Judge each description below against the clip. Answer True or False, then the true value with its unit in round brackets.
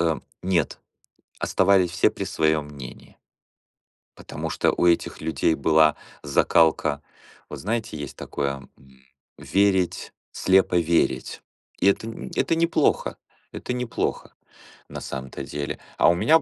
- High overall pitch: False (85 Hz)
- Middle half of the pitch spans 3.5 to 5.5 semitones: True (4.8 semitones)